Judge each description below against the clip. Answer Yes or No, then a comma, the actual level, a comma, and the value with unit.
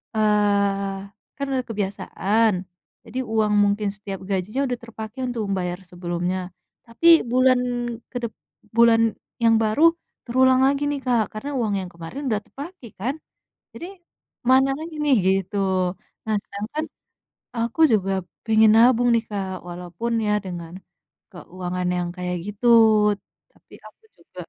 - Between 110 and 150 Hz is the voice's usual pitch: No, high, 215 Hz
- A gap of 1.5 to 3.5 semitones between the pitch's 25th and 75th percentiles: No, average, 4.1 semitones